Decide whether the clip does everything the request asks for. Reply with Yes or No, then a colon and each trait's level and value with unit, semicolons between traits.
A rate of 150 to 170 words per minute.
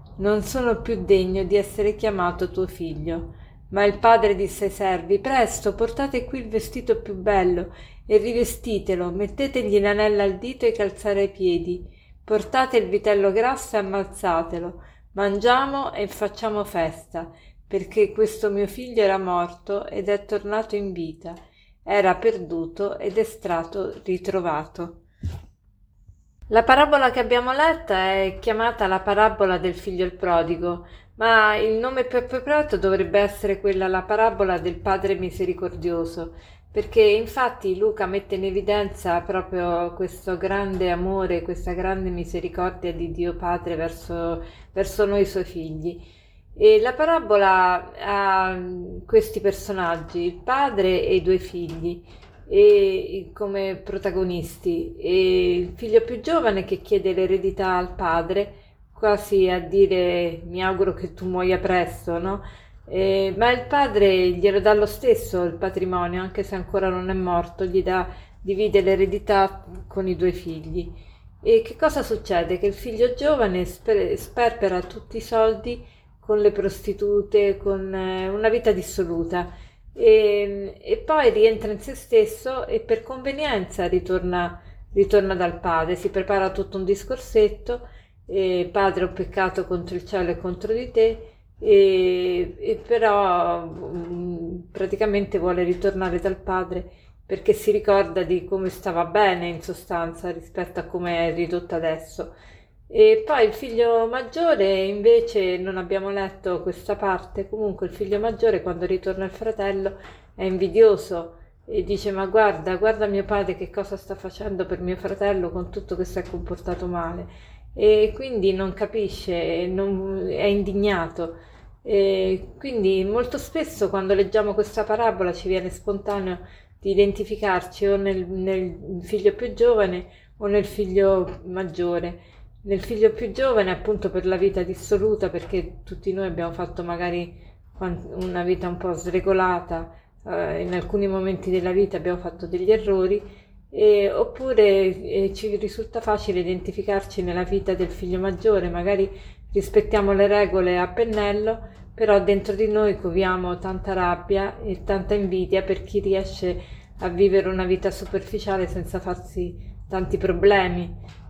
No: average, 140 wpm